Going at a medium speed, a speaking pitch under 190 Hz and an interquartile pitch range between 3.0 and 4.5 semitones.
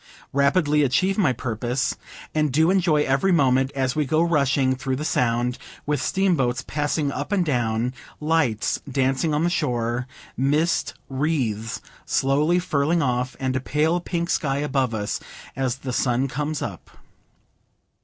Yes: average, 145 wpm; medium, 140 Hz; average, 3.5 semitones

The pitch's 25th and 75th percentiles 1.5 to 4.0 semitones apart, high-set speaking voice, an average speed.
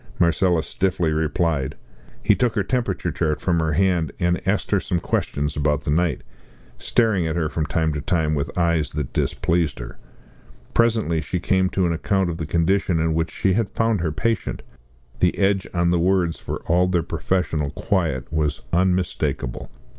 No: average, 3.1 semitones; very low, 85 Hz; average, 175 wpm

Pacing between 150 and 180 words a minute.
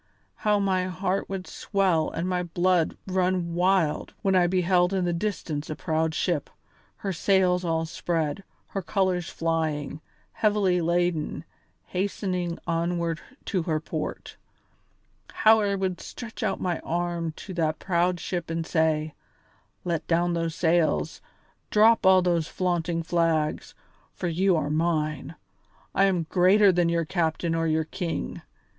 No: average, 140 wpm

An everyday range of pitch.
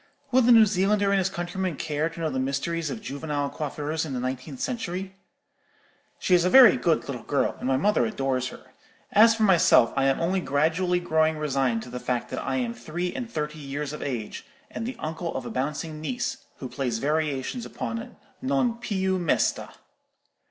No: wide, 5.9 semitones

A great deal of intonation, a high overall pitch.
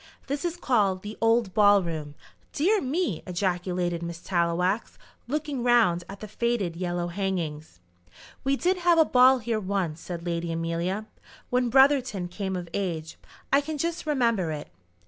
Yes: wide, 6.6 semitones; high, 200 Hz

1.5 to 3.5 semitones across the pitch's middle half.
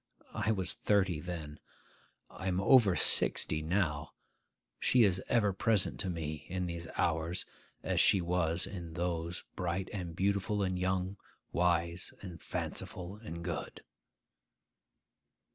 Yes: narrow, 2.4 semitones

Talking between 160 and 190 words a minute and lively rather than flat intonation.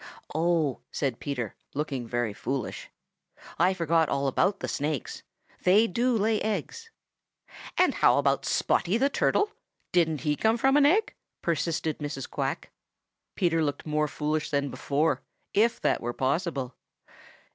No: average, 140 wpm; wide, 6.1 semitones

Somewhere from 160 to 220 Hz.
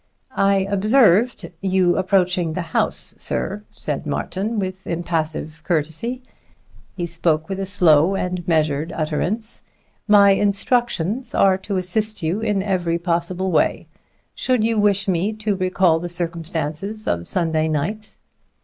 Yes: medium, 185 Hz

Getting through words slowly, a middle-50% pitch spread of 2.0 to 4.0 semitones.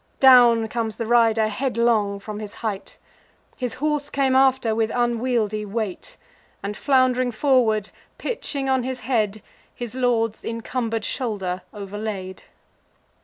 Yes: slow, 120 wpm; average, 3.0 semitones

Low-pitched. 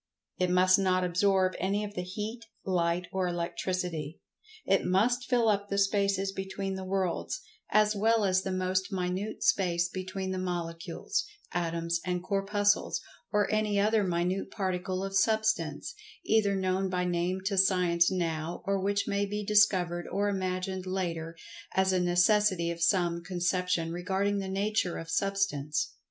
No: medium, 185 Hz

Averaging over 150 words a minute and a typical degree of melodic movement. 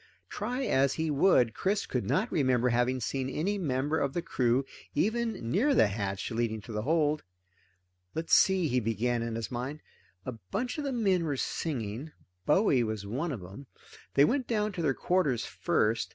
No: average, 180 wpm; wide, 7.7 semitones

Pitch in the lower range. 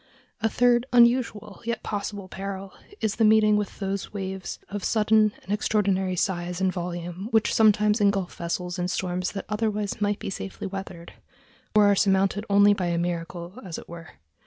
No: high, 200 Hz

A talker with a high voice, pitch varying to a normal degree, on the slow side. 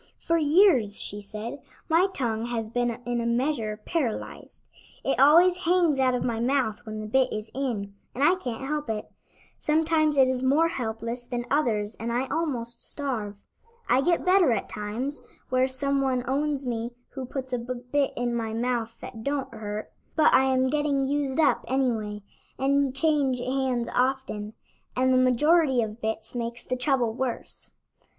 No: very high, 255 Hz; average, 3.4 semitones; average, 170 wpm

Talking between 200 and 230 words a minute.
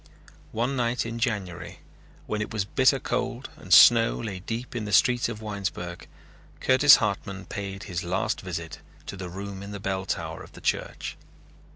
No: average, 175 wpm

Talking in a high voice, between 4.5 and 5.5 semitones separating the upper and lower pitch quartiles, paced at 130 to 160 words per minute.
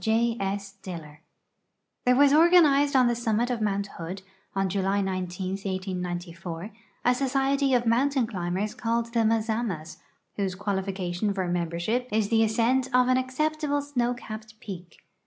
Yes: high, 220 Hz; average, 4.9 semitones; average, 140 wpm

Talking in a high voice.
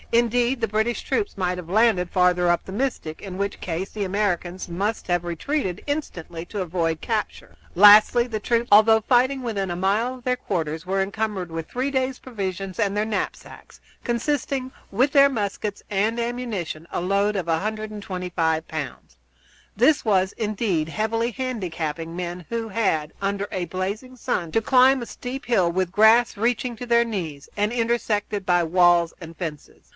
Yes: high, 205 Hz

